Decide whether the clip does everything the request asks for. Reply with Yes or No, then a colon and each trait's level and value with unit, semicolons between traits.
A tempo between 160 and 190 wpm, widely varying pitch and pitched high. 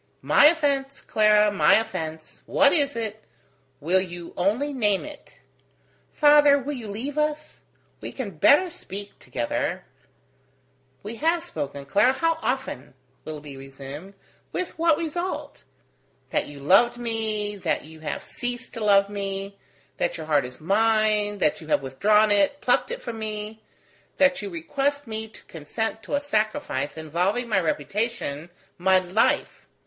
No: average, 150 wpm; wide, 7.4 semitones; high, 215 Hz